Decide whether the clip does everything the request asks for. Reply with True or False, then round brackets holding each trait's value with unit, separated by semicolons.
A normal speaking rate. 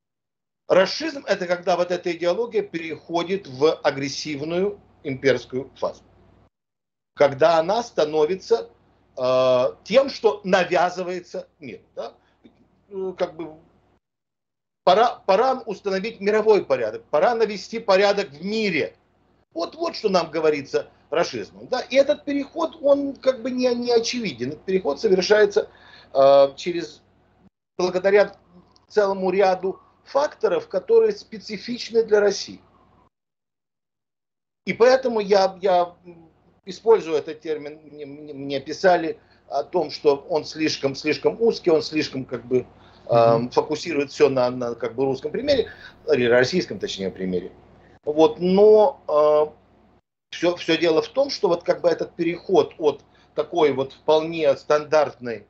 True (120 wpm)